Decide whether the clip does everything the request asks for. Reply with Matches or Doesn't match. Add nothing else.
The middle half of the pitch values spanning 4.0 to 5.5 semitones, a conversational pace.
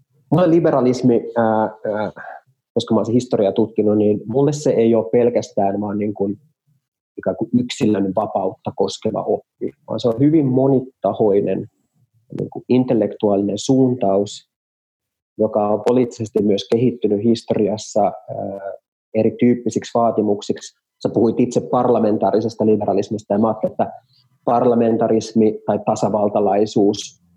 Doesn't match